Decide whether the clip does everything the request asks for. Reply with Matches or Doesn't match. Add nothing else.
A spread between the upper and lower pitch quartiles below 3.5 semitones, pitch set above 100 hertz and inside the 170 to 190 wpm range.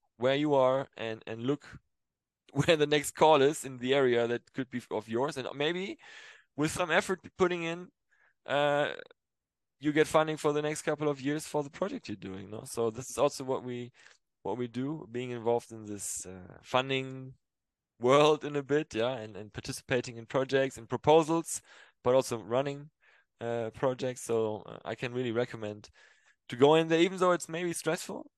Doesn't match